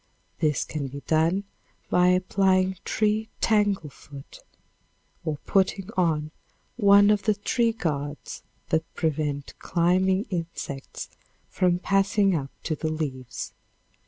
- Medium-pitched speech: Yes, medium, 180 Hz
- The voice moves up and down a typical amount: Yes, average, 4.4 semitones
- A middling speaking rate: No, slow, 110 wpm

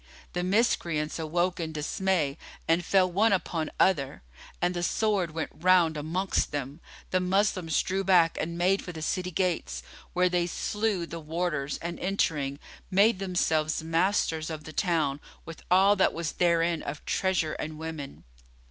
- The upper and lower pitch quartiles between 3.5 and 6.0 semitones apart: No, average, 2.8 semitones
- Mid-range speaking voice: Yes, medium, 170 Hz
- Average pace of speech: Yes, average, 155 wpm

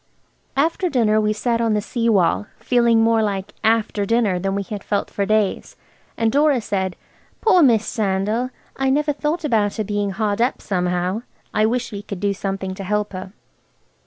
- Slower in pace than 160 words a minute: No, average, 185 wpm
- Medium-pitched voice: No, high, 215 Hz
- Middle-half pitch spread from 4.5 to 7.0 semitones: No, average, 3.0 semitones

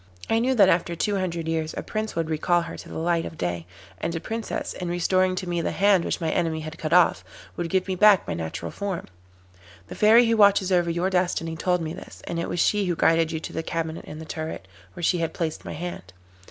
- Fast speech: Yes, fast, 245 wpm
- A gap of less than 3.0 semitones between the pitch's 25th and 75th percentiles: Yes, narrow, 2.5 semitones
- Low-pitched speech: No, medium, 170 Hz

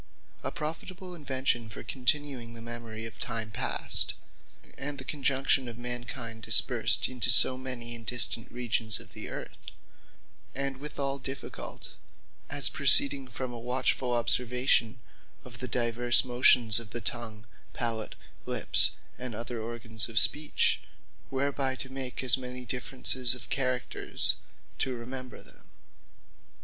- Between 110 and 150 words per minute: Yes, slow, 135 wpm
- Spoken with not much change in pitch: Yes, narrow, 2.1 semitones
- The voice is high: No, low, 125 Hz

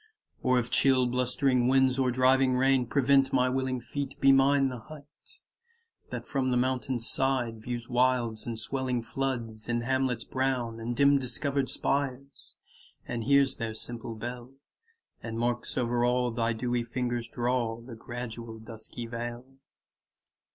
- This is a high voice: No, low, 125 Hz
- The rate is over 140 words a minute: Yes, average, 150 wpm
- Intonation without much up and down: Yes, narrow, 2.1 semitones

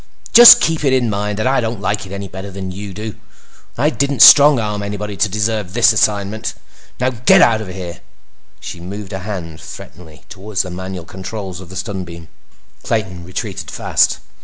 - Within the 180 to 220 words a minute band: Yes, average, 185 wpm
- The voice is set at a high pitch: No, low, 100 Hz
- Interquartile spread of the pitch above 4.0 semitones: No, average, 3.0 semitones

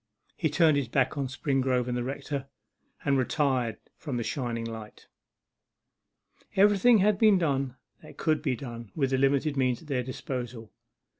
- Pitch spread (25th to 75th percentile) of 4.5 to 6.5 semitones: No, average, 3.3 semitones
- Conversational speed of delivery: Yes, average, 160 wpm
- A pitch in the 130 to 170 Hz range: Yes, low, 135 Hz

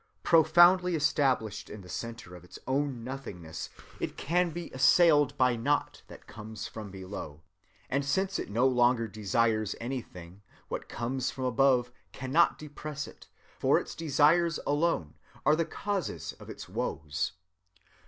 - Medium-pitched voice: No, low, 130 Hz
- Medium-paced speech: Yes, average, 145 wpm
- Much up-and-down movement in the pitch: Yes, wide, 5.8 semitones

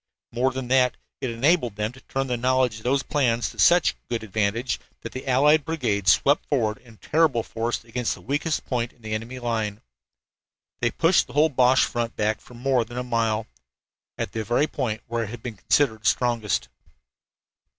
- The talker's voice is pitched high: No, low, 120 Hz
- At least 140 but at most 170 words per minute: No, average, 190 wpm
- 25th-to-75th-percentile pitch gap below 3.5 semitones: Yes, average, 2.8 semitones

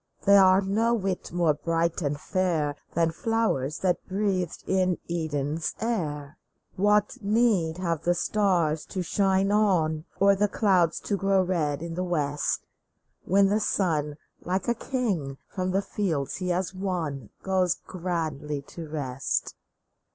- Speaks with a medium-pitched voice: Yes, medium, 180 Hz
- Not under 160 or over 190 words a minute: No, average, 145 wpm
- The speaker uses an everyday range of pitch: Yes, average, 3.8 semitones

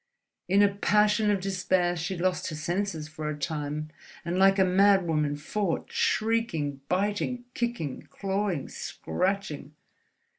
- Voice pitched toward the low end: No, medium, 185 Hz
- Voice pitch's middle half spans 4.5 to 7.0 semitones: Yes, average, 4.8 semitones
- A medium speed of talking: No, slow, 125 wpm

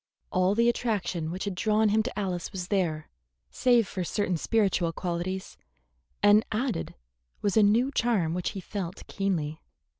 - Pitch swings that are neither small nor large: Yes, average, 3.4 semitones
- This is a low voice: No, high, 195 Hz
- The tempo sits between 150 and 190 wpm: Yes, average, 155 wpm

